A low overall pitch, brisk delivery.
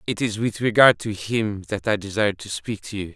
Yes: low, 105 Hz; fast, 245 wpm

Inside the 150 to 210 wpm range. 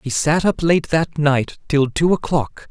Yes: average, 200 wpm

